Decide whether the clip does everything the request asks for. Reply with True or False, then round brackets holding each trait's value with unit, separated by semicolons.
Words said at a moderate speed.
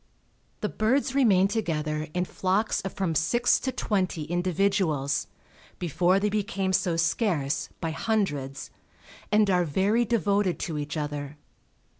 False (130 wpm)